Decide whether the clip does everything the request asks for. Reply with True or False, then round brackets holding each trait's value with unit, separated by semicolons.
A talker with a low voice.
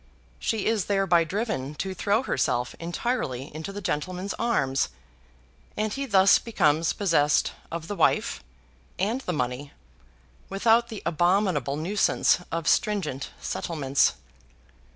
False (180 Hz)